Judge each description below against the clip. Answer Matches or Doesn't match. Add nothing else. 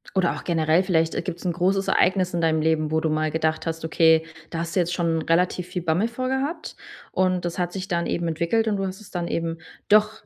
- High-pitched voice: Doesn't match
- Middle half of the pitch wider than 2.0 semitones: Matches